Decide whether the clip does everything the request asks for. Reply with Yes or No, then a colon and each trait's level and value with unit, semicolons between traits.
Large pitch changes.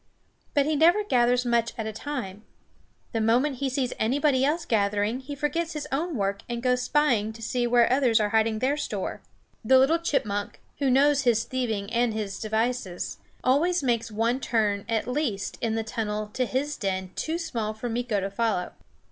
No: average, 4.1 semitones